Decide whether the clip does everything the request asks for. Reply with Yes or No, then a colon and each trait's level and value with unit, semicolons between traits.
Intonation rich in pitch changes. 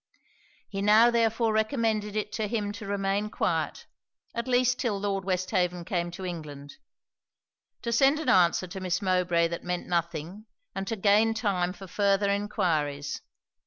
No: average, 3.5 semitones